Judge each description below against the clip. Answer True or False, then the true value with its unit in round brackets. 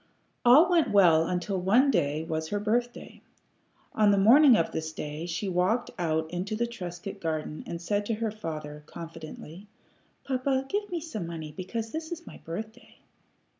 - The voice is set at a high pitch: True (195 Hz)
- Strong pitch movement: True (6.4 semitones)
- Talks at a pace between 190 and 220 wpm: False (170 wpm)